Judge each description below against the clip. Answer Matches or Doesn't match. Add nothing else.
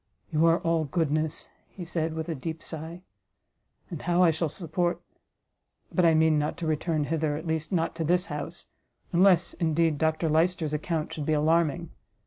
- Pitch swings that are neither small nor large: Doesn't match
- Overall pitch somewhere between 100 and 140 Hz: Doesn't match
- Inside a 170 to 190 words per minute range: Matches